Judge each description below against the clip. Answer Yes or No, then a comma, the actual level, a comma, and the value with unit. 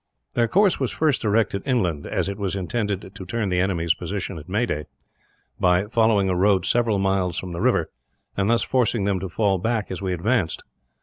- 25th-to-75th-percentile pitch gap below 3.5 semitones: No, average, 3.8 semitones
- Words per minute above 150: Yes, average, 195 wpm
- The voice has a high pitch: No, low, 100 Hz